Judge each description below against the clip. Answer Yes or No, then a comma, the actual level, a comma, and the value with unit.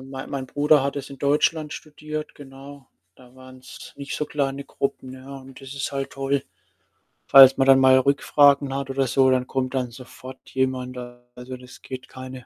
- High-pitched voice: No, low, 135 Hz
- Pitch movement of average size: No, narrow, 1.3 semitones